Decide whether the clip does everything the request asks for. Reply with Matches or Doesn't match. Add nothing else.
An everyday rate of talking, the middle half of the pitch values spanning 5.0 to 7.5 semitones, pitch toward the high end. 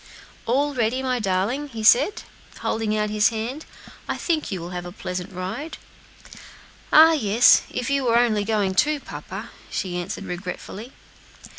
Matches